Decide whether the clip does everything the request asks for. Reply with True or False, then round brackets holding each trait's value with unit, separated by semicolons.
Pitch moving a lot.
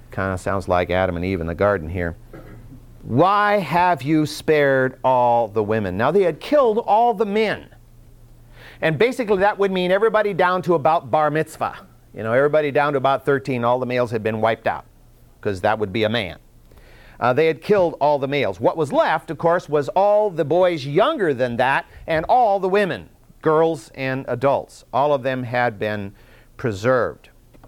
True (6.4 semitones)